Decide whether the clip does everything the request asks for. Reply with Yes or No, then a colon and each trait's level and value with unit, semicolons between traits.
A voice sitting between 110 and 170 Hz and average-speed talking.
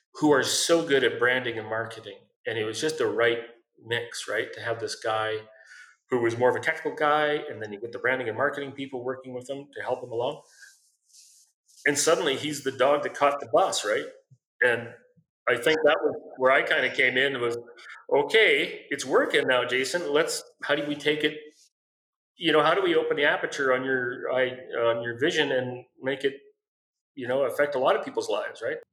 No: medium, 140 Hz; fast, 210 wpm